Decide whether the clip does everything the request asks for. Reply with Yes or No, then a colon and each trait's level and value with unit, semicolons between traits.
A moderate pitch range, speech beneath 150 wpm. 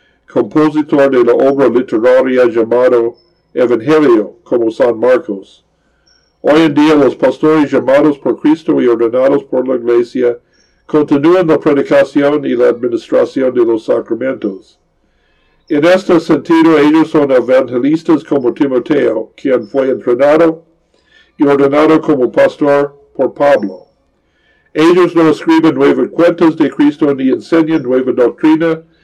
Yes: average, 4.1 semitones; slow, 125 wpm